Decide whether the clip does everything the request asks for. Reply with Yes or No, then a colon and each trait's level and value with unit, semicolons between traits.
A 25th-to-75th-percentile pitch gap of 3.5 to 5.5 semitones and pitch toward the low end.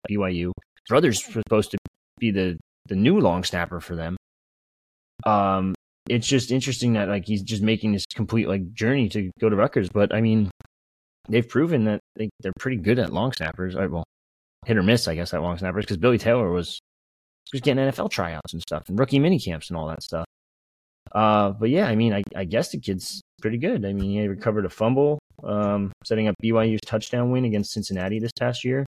Yes: average, 4.3 semitones; low, 105 Hz